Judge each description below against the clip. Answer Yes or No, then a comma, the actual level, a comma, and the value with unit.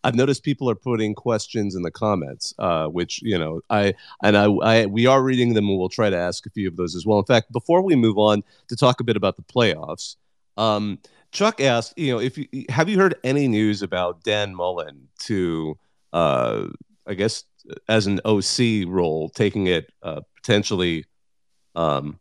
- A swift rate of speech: No, average, 190 wpm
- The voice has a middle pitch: No, low, 105 Hz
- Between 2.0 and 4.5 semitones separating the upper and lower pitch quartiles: No, average, 4.9 semitones